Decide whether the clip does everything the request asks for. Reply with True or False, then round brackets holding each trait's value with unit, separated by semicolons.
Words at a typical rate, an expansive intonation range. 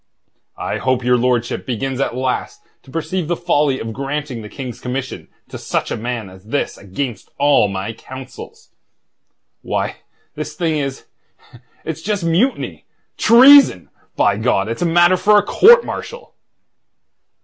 True (145 wpm; 6.3 semitones)